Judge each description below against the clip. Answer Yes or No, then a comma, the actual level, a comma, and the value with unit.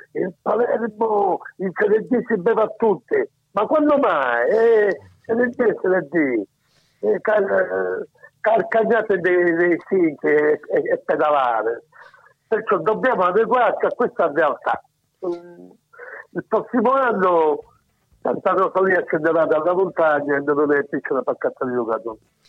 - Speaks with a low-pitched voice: No, high, 220 Hz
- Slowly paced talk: No, average, 125 wpm